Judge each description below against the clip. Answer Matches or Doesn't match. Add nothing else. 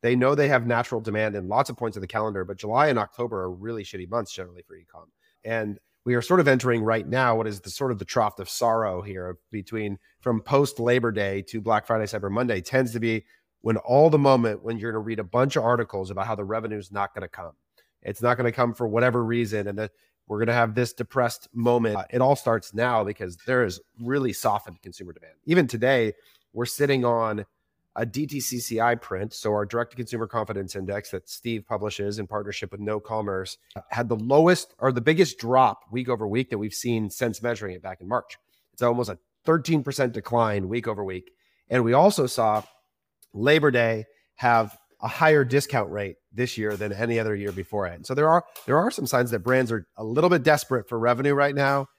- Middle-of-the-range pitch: Doesn't match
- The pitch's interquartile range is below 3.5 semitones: Matches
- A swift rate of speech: Matches